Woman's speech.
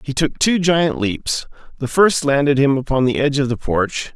No: male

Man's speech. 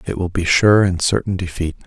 Yes: male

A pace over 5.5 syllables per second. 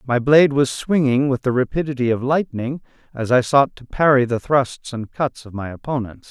No: 5.1 syllables/s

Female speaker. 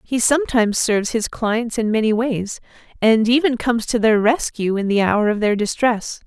Yes: female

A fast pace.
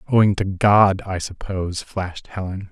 No: average, 155 wpm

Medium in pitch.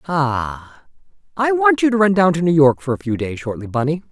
Yes: medium, 160 Hz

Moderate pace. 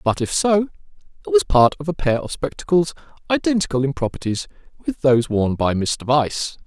Yes: average, 180 wpm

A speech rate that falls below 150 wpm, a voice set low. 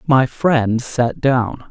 Yes: average, 140 wpm; low, 125 Hz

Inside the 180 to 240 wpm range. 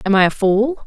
No: fast, 280 wpm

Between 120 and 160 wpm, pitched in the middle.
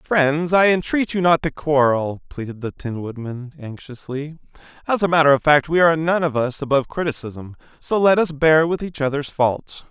No: average, 195 wpm; medium, 150 Hz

